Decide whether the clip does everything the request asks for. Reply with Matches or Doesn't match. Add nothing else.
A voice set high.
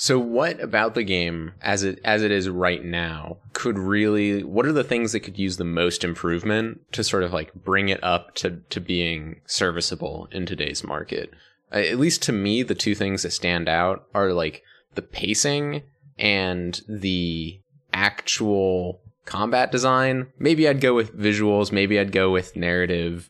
Doesn't match